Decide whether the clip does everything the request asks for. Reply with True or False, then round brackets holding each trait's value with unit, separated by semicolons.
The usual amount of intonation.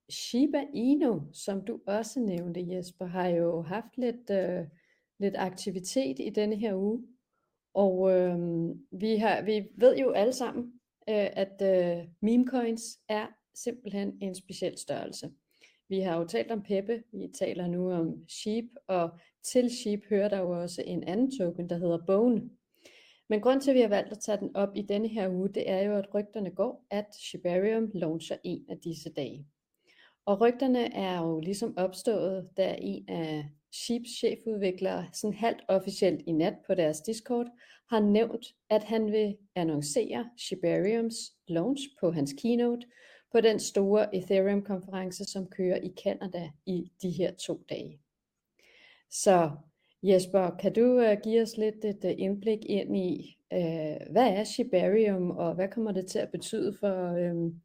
True (4.0 semitones)